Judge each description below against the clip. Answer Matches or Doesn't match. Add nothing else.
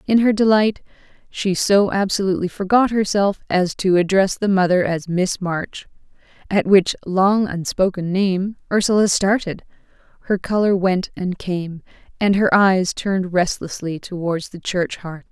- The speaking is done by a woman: Matches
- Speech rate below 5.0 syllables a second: Matches